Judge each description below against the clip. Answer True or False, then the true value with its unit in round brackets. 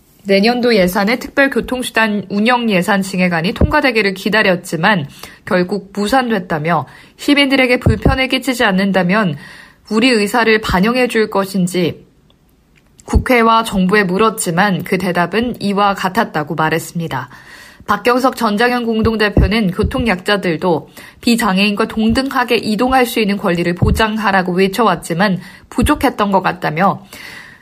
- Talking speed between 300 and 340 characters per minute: True (310 characters per minute)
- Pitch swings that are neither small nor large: True (4.0 semitones)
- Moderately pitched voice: False (210 Hz)